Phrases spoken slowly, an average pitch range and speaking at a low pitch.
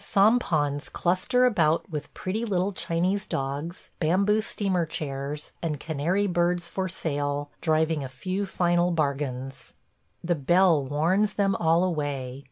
No: slow, 130 wpm; average, 4.4 semitones; medium, 170 Hz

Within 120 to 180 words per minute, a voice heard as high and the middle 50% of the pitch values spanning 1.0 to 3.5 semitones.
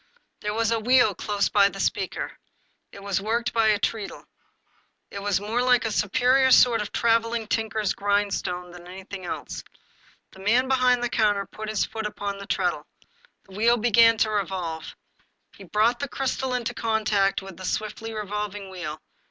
Yes: average, 175 wpm; high, 210 Hz; narrow, 2.6 semitones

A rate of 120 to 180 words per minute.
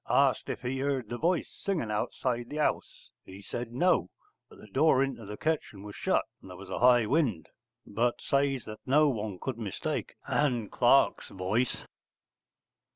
Yes: average, 170 wpm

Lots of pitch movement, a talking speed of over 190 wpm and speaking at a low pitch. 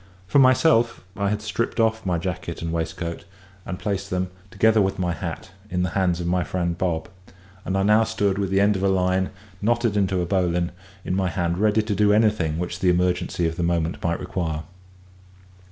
No: average, 2.9 semitones; average, 200 wpm; very low, 95 Hz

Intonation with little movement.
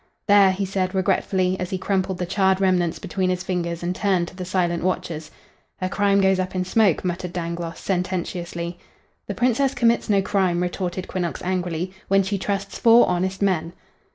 Yes: narrow, 1.8 semitones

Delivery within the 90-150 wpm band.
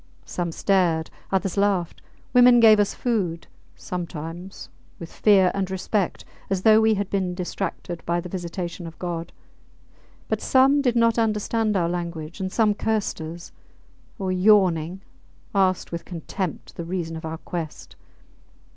Yes: average, 145 wpm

